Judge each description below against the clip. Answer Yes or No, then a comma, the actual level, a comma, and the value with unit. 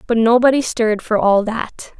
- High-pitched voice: Yes, high, 235 Hz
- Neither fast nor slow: Yes, average, 180 wpm